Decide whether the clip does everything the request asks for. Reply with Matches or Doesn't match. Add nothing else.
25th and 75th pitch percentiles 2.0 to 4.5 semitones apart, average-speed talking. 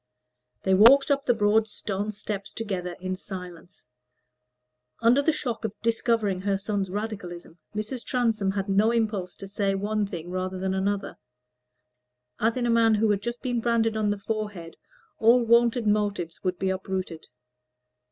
Matches